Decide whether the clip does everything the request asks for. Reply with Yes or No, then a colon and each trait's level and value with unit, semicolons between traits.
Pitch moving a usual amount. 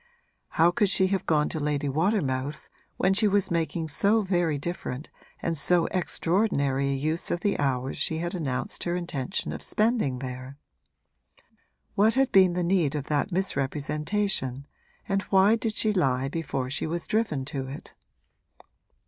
No: wide, 5.7 semitones